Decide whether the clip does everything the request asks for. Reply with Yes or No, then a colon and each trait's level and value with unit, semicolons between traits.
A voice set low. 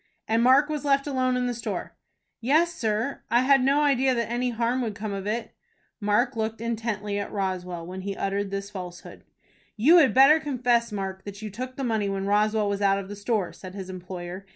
No: high, 220 Hz